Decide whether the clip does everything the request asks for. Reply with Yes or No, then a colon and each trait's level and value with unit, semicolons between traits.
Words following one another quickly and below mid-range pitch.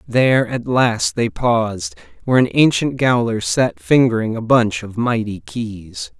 No: average, 155 wpm; low, 110 Hz